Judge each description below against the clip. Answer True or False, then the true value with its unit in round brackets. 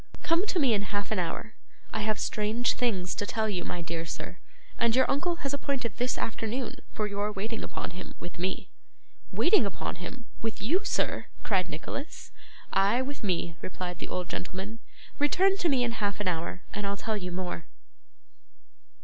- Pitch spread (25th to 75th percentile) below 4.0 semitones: False (5.1 semitones)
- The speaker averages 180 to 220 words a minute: True (185 wpm)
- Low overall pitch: False (210 Hz)